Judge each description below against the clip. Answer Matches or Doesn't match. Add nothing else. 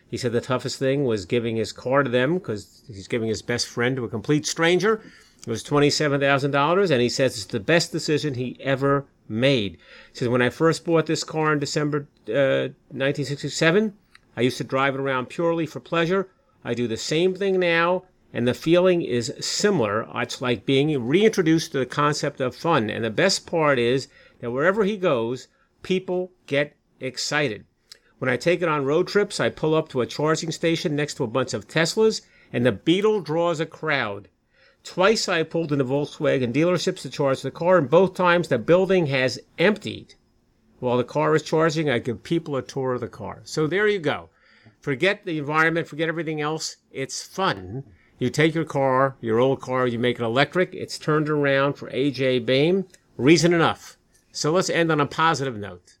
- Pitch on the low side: Doesn't match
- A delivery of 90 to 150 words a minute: Doesn't match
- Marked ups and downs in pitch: Doesn't match